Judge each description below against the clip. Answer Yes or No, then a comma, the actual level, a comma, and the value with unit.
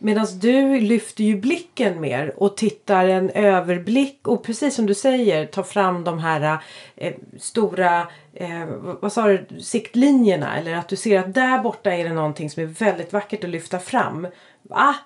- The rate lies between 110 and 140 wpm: No, average, 175 wpm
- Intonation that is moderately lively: Yes, average, 4.5 semitones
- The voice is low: No, high, 200 Hz